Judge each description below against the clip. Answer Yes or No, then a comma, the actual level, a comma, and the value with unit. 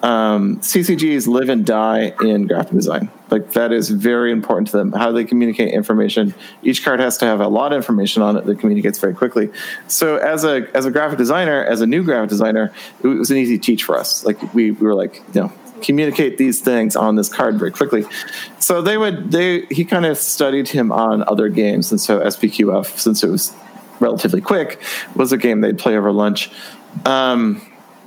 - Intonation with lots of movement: Yes, wide, 6.4 semitones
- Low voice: Yes, low, 120 Hz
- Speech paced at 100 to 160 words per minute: No, fast, 205 wpm